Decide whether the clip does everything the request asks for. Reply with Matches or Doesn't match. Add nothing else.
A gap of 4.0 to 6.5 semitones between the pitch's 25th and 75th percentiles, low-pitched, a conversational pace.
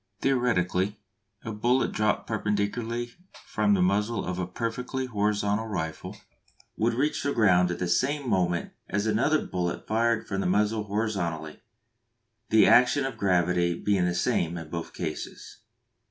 Matches